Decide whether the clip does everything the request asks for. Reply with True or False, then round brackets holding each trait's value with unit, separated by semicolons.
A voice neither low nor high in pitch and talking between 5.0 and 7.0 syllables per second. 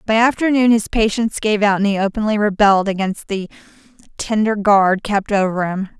False (205 Hz; 5.5 syllables/s)